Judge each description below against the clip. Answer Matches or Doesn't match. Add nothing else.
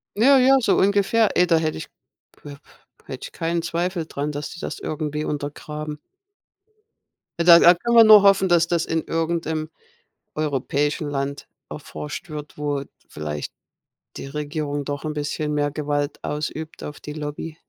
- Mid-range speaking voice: Matches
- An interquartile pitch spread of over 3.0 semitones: Doesn't match